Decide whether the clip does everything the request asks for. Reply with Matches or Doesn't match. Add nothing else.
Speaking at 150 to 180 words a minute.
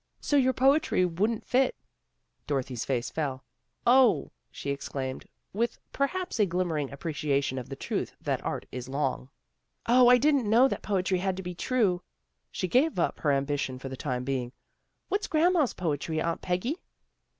Matches